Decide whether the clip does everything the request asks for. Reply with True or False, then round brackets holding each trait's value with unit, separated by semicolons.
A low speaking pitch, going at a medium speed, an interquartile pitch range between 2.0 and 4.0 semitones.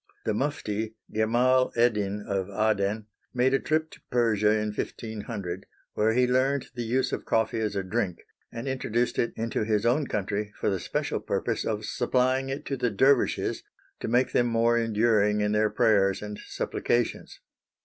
True (110 Hz; 170 wpm; 2.8 semitones)